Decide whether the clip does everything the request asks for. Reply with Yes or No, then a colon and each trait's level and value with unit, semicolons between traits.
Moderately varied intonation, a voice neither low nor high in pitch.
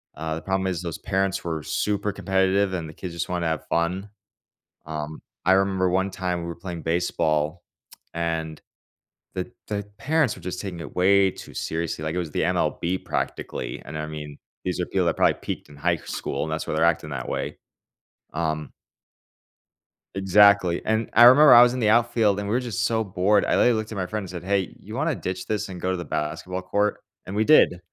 No: average, 3.5 semitones; very low, 90 Hz